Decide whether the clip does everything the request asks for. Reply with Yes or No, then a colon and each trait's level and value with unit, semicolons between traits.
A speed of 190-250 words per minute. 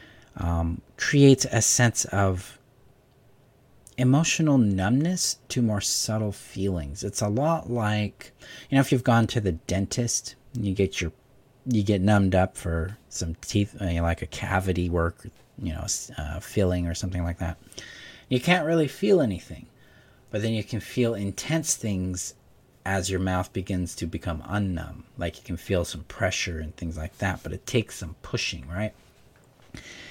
No: average, 160 wpm